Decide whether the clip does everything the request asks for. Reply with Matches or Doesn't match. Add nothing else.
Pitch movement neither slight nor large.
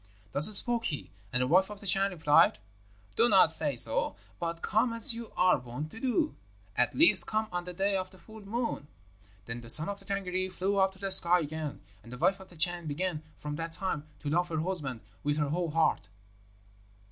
Matches